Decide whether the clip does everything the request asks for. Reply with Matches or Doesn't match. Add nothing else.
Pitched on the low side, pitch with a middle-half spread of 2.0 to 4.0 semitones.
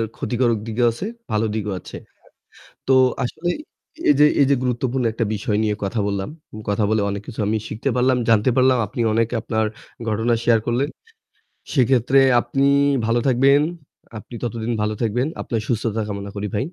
Matches